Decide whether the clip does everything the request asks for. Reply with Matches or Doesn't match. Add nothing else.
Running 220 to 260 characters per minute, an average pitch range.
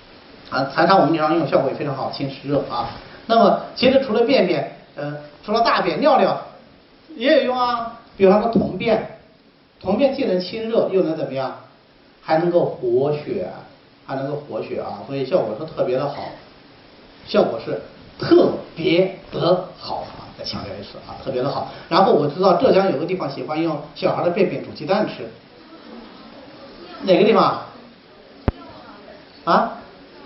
Doesn't match